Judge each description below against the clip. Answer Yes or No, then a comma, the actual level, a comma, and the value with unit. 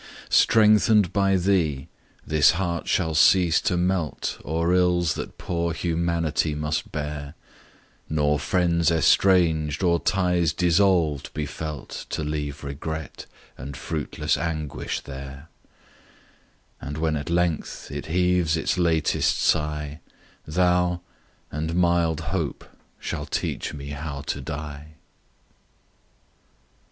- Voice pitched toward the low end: Yes, very low, 80 Hz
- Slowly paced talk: Yes, slow, 110 wpm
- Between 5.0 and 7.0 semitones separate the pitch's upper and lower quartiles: No, average, 2.7 semitones